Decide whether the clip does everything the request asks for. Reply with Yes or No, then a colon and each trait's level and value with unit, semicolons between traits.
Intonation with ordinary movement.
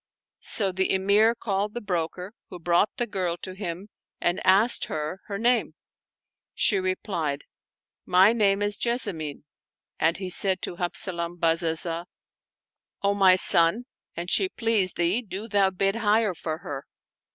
Yes: average, 3.2 semitones